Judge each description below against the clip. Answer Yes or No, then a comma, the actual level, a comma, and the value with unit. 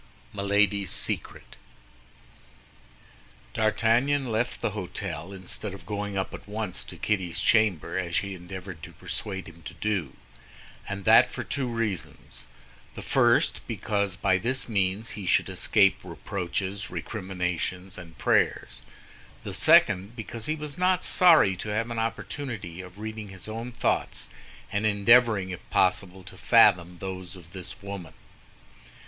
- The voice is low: Yes, low, 100 Hz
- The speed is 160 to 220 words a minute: No, slow, 135 wpm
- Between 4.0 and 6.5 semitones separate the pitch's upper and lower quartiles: No, average, 3.2 semitones